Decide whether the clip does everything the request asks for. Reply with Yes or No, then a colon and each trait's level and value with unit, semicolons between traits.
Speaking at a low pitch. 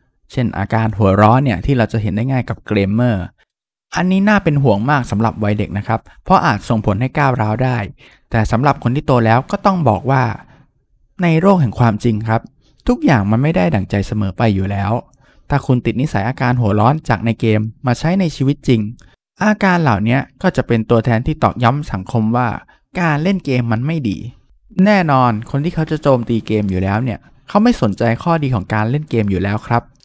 Yes: low, 120 Hz